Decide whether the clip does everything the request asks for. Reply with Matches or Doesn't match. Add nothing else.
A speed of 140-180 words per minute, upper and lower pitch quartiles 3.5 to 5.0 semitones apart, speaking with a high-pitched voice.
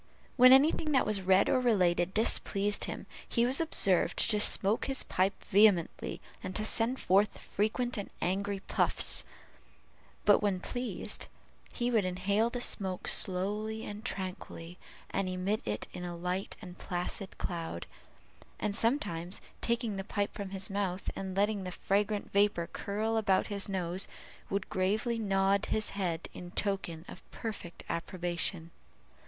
Doesn't match